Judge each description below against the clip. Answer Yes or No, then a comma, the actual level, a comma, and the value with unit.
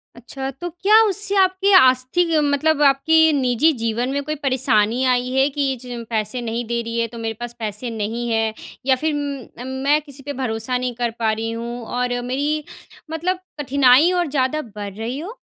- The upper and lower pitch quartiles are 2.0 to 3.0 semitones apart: No, average, 4.2 semitones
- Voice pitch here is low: No, very high, 255 Hz